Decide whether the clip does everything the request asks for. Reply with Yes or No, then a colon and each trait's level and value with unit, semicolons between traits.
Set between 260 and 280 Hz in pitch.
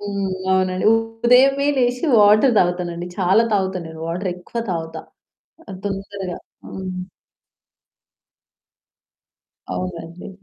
No: high, 190 Hz